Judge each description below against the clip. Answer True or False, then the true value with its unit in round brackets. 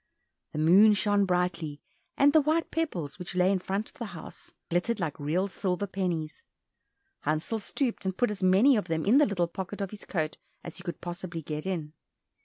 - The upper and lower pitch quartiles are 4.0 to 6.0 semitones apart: False (3.5 semitones)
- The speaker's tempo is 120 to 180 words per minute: False (200 wpm)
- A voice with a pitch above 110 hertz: True (185 Hz)